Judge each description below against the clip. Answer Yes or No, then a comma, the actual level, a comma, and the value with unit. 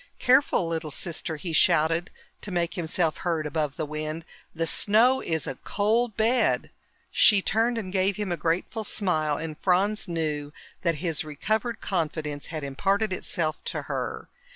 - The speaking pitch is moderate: Yes, medium, 170 Hz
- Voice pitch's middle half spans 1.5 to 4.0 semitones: No, average, 4.6 semitones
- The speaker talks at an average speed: Yes, average, 155 wpm